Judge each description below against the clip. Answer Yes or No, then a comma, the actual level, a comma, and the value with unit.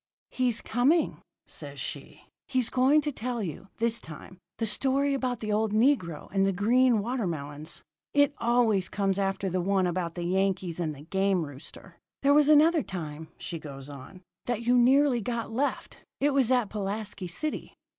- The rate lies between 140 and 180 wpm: Yes, average, 170 wpm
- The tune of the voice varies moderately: No, wide, 5.9 semitones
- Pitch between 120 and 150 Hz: No, high, 215 Hz